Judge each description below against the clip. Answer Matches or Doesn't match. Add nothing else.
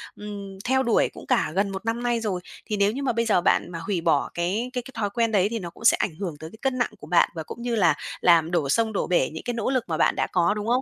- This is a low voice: Doesn't match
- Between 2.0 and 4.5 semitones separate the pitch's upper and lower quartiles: Doesn't match